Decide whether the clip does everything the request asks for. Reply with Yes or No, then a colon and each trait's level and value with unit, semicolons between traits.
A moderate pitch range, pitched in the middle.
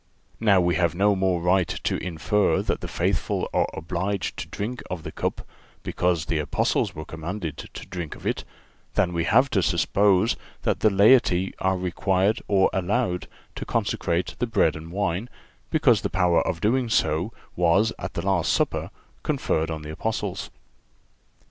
No: average, 3.3 semitones; very low, 95 Hz